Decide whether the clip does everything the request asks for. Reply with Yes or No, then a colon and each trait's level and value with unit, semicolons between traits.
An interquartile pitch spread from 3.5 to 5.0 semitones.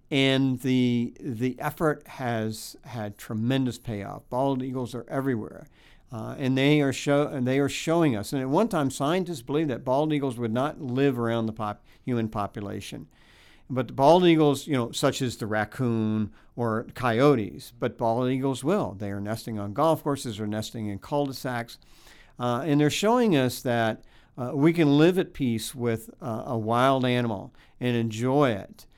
Yes: average, 3.8 semitones